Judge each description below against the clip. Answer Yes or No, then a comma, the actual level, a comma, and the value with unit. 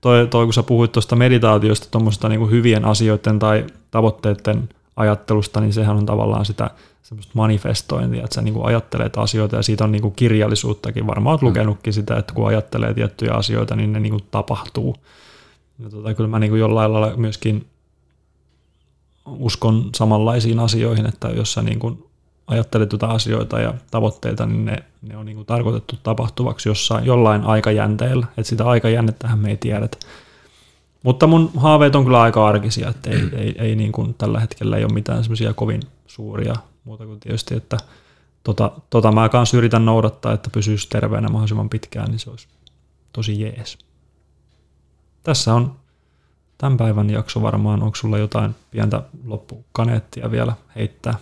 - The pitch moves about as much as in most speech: No, narrow, 1.7 semitones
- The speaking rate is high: Yes, fast, 160 wpm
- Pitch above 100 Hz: Yes, low, 110 Hz